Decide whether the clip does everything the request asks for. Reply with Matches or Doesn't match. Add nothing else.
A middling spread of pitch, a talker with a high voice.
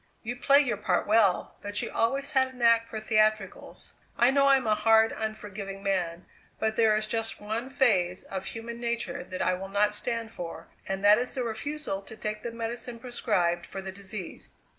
Matches